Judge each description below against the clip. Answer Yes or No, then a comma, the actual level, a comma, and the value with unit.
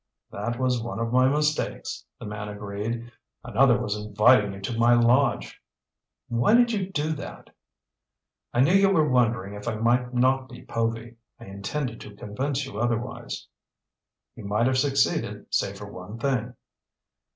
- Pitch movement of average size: Yes, average, 3.7 semitones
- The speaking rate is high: No, average, 160 wpm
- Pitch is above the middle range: No, low, 120 Hz